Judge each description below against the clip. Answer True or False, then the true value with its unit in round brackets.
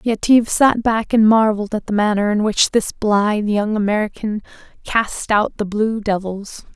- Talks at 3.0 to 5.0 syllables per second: True (4.7 syllables/s)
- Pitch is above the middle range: True (215 Hz)